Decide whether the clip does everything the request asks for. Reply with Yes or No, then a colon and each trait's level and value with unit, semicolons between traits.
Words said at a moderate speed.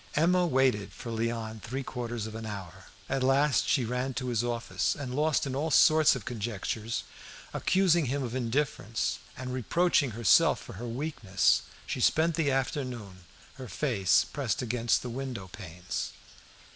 Yes: average, 160 wpm